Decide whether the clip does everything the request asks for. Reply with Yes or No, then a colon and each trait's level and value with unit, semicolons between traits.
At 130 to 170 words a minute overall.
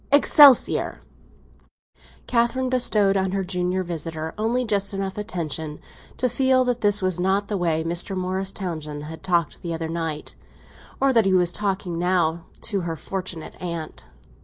Yes: average, 155 wpm